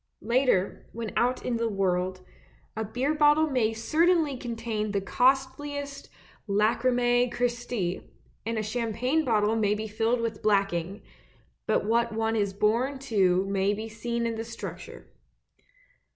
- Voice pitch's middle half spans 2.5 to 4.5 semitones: Yes, average, 3.0 semitones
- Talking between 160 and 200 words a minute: No, slow, 135 wpm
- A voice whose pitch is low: No, high, 230 Hz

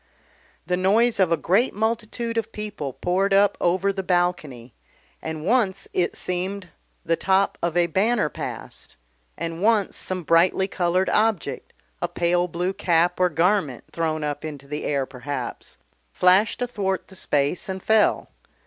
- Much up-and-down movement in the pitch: No, average, 3.3 semitones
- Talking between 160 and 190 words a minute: No, average, 150 wpm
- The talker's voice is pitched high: No, medium, 180 Hz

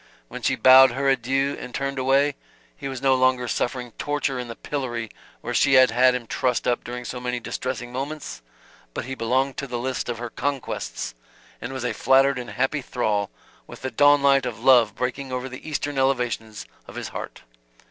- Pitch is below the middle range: Yes, low, 130 Hz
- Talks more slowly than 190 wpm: No, average, 200 wpm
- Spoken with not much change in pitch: Yes, narrow, 1.8 semitones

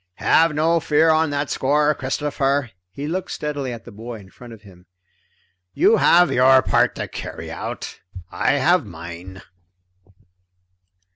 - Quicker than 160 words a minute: No, average, 145 wpm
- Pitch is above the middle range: No, medium, 140 Hz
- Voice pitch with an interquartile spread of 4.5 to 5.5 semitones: Yes, average, 5.1 semitones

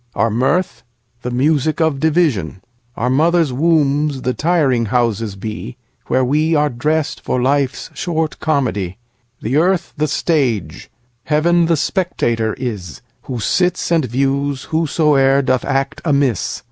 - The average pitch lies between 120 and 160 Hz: Yes, low, 135 Hz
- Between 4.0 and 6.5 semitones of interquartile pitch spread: Yes, average, 4.6 semitones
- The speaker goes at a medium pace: No, slow, 120 wpm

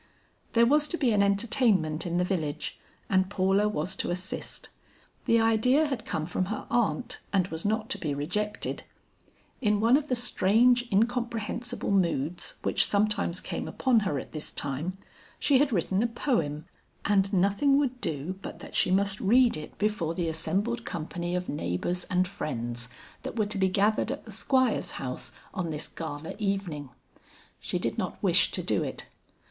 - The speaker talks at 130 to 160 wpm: No, average, 175 wpm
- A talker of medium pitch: No, high, 200 Hz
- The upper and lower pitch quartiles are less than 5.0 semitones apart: No, average, 5.3 semitones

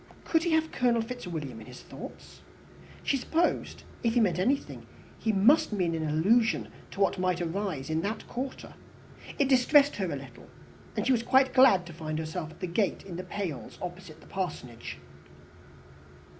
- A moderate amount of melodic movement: No, wide, 7.3 semitones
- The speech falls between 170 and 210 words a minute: Yes, average, 175 wpm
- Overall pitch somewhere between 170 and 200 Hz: Yes, high, 190 Hz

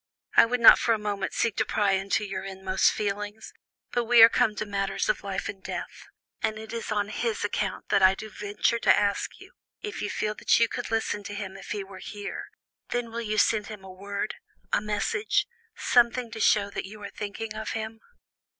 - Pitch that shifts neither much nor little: No, narrow, 2.0 semitones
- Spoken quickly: Yes, fast, 215 wpm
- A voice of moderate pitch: No, high, 210 Hz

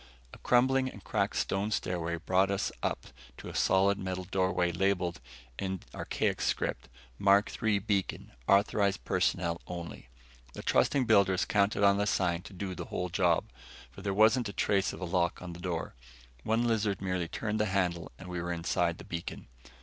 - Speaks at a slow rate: No, average, 180 wpm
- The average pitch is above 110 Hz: No, very low, 95 Hz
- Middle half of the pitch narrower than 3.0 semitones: Yes, narrow, 2.4 semitones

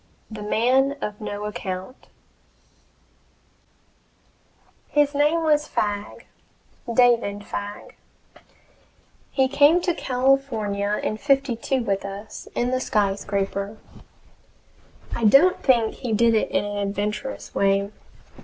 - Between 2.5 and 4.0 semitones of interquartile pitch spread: No, average, 4.7 semitones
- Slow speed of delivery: Yes, slow, 105 wpm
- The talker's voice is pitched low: No, high, 220 Hz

